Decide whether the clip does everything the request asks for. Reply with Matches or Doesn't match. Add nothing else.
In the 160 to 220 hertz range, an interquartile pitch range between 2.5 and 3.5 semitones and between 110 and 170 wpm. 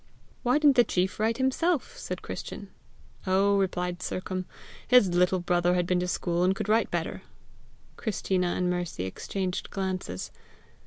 Matches